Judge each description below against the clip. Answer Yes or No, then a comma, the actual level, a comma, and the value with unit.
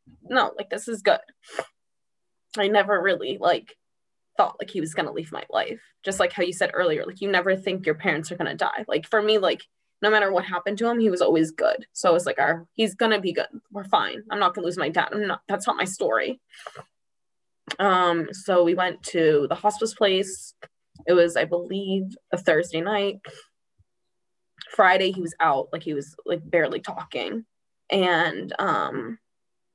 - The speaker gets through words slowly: No, average, 195 wpm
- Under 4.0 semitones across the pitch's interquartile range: Yes, average, 3.2 semitones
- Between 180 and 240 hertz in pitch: Yes, high, 190 Hz